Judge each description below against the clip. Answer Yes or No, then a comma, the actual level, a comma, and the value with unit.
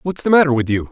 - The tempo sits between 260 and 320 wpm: No, fast, 330 wpm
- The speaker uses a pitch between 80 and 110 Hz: No, medium, 140 Hz